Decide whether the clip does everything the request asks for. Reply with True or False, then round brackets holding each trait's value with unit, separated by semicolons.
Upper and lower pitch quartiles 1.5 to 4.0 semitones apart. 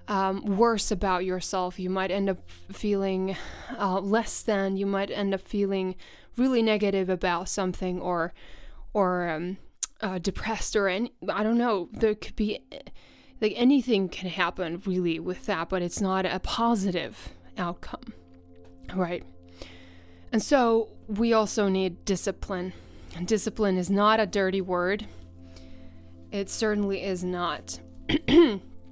True (3.2 semitones)